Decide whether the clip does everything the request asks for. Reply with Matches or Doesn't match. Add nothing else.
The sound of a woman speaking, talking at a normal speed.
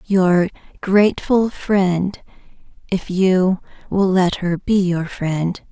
Doesn't match